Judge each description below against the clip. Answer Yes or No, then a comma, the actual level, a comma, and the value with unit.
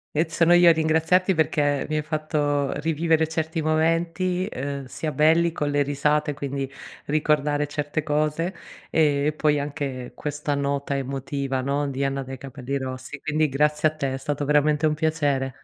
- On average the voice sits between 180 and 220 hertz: No, medium, 150 Hz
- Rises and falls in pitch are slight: Yes, narrow, 2.1 semitones